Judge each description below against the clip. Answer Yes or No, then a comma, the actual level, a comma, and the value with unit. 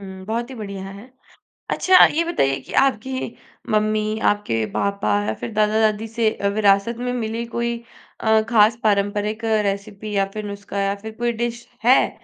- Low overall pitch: No, high, 215 Hz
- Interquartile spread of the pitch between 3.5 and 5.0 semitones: No, average, 2.8 semitones